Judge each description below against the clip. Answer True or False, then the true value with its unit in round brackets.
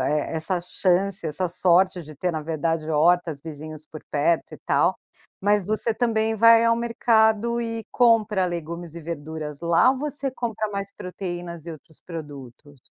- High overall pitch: False (175 Hz)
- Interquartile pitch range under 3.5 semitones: False (5.6 semitones)